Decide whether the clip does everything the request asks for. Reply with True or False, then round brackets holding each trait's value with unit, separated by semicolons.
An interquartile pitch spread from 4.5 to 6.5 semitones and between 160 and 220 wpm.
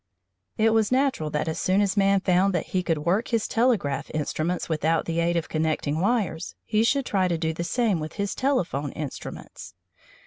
True (5.1 semitones; 195 wpm)